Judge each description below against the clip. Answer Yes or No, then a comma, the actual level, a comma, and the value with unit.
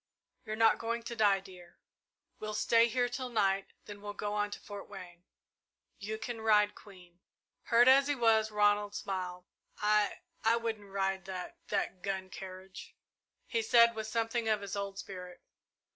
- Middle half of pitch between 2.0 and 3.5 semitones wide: Yes, average, 2.8 semitones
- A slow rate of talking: No, average, 165 wpm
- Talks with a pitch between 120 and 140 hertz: No, high, 210 Hz